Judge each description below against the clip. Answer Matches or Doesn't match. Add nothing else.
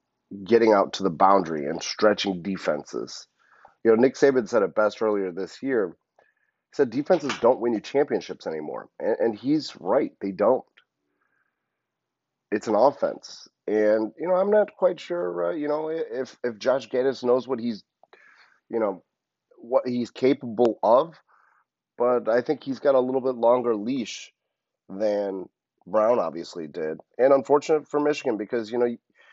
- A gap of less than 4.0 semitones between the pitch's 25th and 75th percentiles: Doesn't match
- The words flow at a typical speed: Matches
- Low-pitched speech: Matches